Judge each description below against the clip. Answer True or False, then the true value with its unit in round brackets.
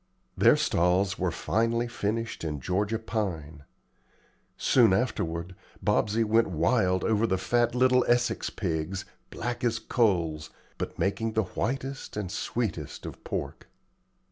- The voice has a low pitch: True (105 Hz)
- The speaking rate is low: True (125 wpm)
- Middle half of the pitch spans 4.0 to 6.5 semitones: True (4.6 semitones)